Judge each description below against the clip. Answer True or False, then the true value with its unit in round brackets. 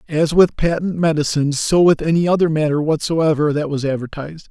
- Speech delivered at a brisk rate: False (175 wpm)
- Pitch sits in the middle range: True (155 Hz)